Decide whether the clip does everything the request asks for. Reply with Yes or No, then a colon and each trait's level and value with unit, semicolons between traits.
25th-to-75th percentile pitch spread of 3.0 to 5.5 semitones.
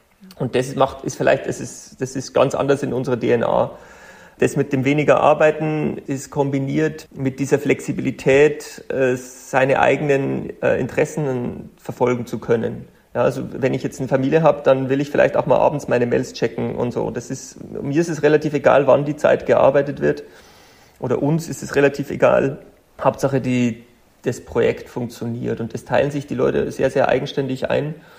No: narrow, 2.5 semitones